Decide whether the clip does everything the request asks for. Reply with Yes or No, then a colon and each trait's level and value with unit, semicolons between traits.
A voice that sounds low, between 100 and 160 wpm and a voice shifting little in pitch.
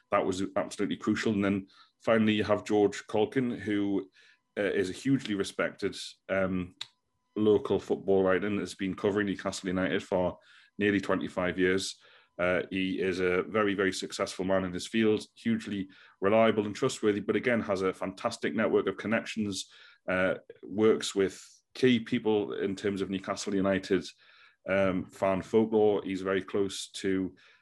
Yes: low, 100 Hz; average, 155 wpm; narrow, 2.0 semitones